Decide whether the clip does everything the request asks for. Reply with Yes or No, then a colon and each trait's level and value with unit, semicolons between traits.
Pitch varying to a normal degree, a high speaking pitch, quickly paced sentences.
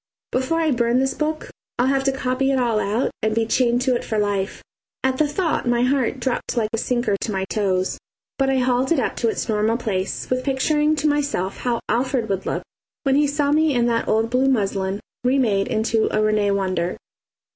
Yes: average, 4.0 semitones; high, 245 Hz; fast, 210 wpm